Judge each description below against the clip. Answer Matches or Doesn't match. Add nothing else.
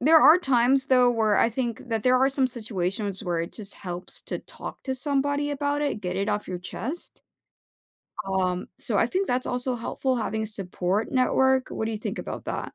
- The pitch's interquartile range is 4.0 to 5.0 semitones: Matches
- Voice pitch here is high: Matches